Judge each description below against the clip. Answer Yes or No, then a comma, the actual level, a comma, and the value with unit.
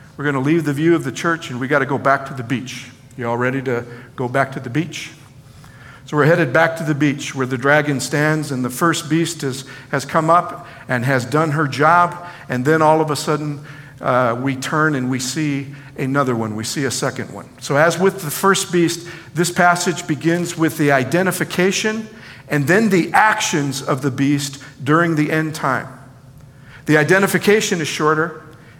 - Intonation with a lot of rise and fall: No, average, 3.4 semitones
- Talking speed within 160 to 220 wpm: Yes, average, 200 wpm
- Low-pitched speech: No, medium, 150 Hz